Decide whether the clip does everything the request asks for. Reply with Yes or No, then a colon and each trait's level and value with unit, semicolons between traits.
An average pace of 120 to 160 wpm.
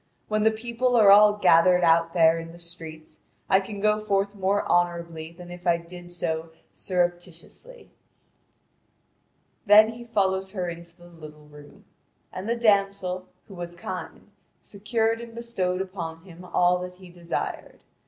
Yes: average, 150 wpm